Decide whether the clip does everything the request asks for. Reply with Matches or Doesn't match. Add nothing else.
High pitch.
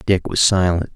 Doesn't match